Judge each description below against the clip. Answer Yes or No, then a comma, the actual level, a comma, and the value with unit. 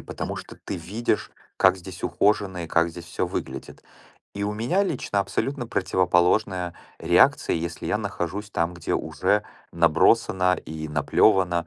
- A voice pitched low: Yes, very low, 90 Hz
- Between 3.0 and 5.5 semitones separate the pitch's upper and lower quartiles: Yes, average, 3.3 semitones